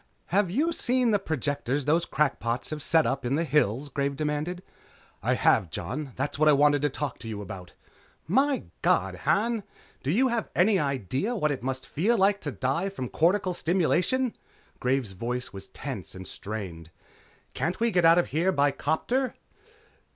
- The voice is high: No, medium, 150 Hz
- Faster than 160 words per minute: Yes, average, 180 wpm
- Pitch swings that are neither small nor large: No, wide, 6.6 semitones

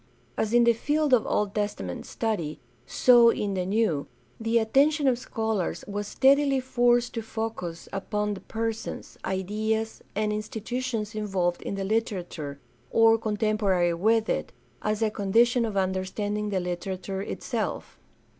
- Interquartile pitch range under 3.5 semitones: Yes, average, 2.9 semitones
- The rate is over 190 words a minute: No, average, 140 wpm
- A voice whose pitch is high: Yes, high, 215 Hz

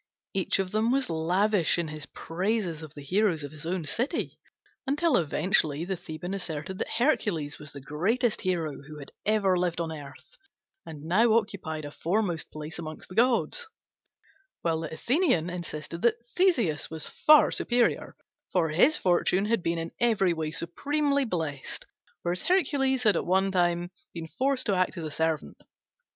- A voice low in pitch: No, medium, 180 Hz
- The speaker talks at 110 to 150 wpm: No, average, 165 wpm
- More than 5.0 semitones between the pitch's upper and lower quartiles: Yes, wide, 5.6 semitones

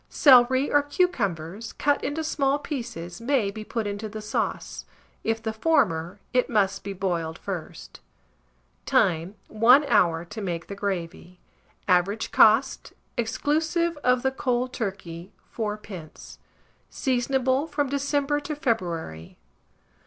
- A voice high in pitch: Yes, high, 225 Hz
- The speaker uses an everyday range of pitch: No, wide, 6.5 semitones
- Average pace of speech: No, slow, 125 wpm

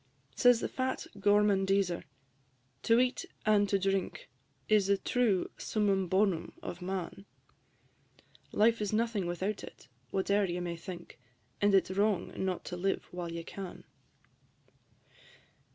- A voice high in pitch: Yes, high, 195 Hz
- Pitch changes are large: No, narrow, 2.5 semitones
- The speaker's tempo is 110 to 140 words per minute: Yes, slow, 135 wpm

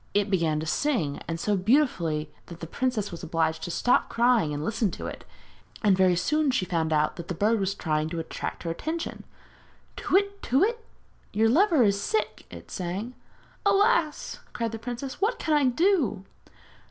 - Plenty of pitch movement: Yes, wide, 8.5 semitones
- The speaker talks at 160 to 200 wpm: Yes, average, 185 wpm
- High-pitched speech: Yes, high, 210 Hz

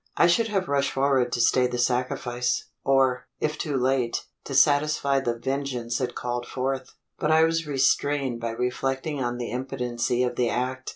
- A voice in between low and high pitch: No, low, 130 Hz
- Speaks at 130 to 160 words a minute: No, average, 175 wpm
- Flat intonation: Yes, narrow, 2.3 semitones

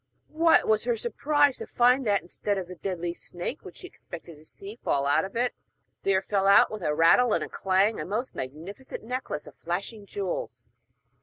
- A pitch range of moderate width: No, wide, 5.7 semitones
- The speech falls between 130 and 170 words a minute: No, average, 200 wpm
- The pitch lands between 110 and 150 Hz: No, high, 200 Hz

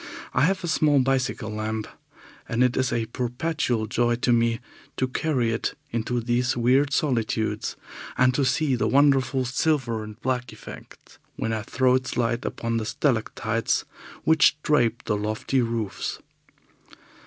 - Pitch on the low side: Yes, low, 125 Hz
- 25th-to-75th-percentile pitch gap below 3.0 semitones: Yes, narrow, 2.6 semitones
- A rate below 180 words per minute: Yes, average, 150 wpm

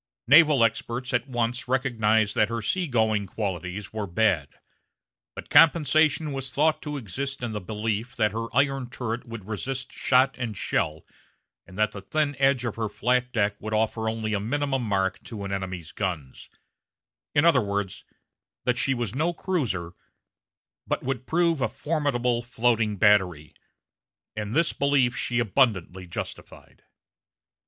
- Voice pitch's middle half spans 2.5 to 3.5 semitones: No, average, 4.5 semitones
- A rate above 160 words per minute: No, average, 150 wpm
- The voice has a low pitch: Yes, low, 115 Hz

